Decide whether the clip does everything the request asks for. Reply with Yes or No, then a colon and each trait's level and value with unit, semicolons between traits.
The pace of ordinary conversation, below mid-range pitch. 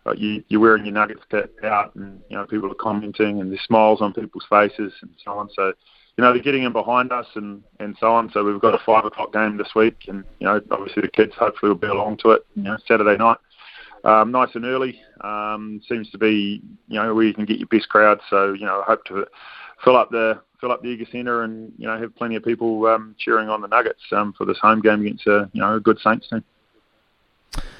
No: fast, 250 wpm; low, 110 Hz